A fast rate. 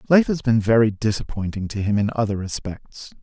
No: average, 185 wpm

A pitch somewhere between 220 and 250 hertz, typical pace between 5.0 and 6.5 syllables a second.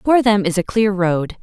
No: high, 200 Hz; 5.8 syllables/s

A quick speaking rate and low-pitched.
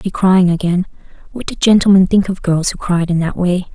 No: fast, 225 wpm; medium, 185 Hz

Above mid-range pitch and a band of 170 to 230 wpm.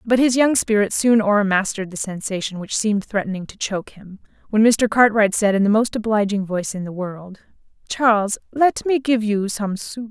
Yes: high, 210 Hz; average, 200 wpm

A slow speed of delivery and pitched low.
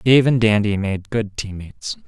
No: average, 200 wpm; low, 105 Hz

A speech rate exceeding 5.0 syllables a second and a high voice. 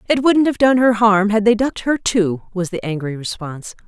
Yes: 5.4 syllables/s; high, 210 Hz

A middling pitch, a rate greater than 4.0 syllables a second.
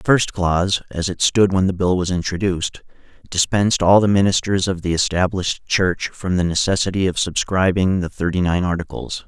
No: very low, 95 Hz; 5.4 syllables/s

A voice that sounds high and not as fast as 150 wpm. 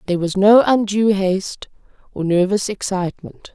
Yes: high, 195 Hz; slow, 135 wpm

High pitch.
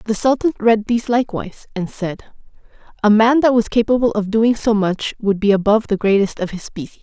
Yes: high, 215 Hz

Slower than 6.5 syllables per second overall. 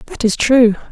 Yes: 5.0 syllables/s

